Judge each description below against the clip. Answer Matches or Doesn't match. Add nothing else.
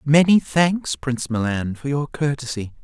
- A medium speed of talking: Matches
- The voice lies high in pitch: Doesn't match